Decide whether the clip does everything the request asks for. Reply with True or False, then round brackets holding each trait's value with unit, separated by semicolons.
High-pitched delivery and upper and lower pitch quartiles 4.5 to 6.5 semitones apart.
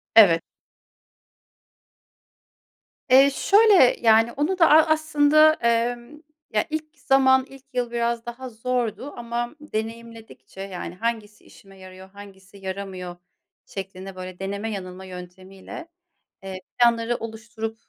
True (230 Hz; 4.9 semitones)